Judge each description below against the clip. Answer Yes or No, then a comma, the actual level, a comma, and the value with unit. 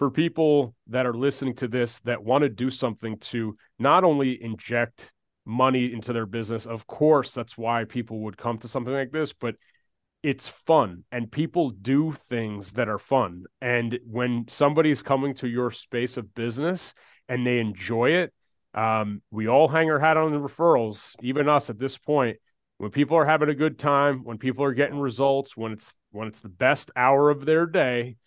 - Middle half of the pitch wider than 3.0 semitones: Yes, average, 3.7 semitones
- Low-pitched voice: Yes, low, 125 Hz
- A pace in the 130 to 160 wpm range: No, average, 190 wpm